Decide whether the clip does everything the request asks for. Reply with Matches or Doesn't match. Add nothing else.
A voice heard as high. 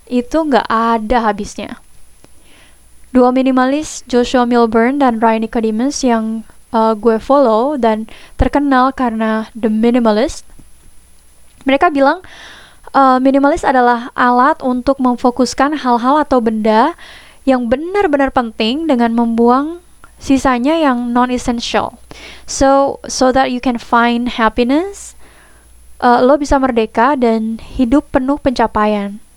Matches